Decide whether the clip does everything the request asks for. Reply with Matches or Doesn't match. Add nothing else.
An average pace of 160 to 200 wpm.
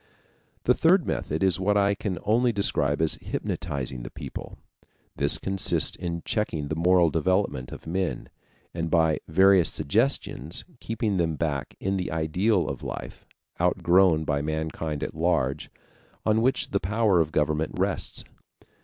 Doesn't match